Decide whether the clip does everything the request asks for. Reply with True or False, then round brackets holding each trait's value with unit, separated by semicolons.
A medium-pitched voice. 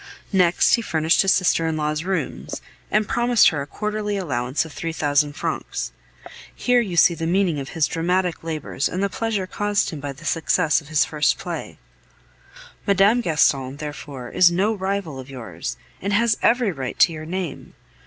True (165 Hz)